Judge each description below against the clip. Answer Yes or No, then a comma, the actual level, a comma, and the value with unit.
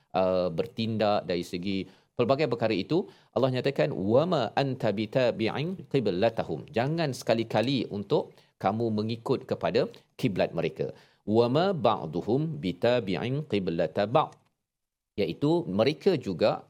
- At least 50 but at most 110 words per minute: Yes, average, 95 wpm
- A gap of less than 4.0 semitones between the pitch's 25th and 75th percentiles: No, wide, 5.5 semitones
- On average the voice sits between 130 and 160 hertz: No, low, 115 Hz